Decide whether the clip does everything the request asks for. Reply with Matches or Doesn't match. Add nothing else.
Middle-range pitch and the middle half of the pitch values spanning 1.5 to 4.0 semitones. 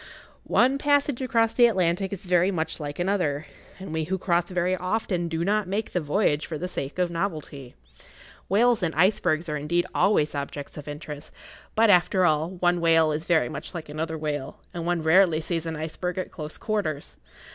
Matches